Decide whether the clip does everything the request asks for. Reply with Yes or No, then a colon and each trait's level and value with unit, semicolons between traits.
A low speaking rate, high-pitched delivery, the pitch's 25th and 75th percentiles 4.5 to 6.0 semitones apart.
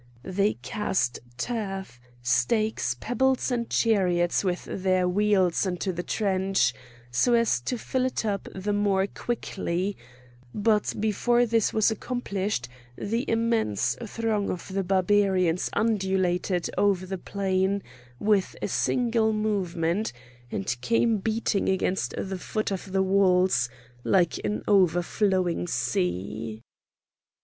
No: slow, 120 wpm; high, 195 Hz; average, 3.2 semitones